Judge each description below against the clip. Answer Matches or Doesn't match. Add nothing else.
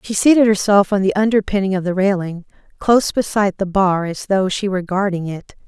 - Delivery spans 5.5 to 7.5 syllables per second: Matches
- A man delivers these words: Doesn't match